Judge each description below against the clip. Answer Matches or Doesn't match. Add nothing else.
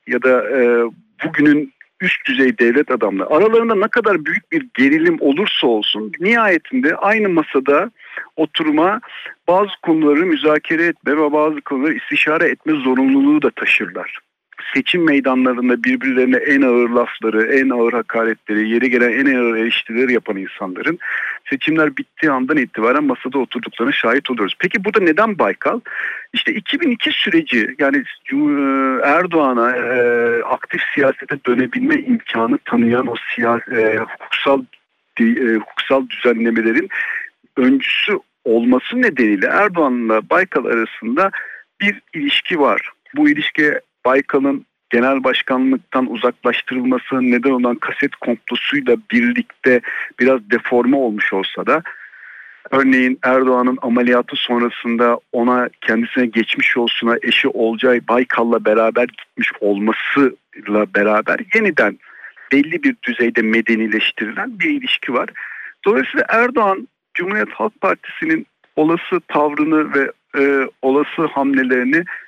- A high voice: Doesn't match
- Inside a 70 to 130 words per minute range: Matches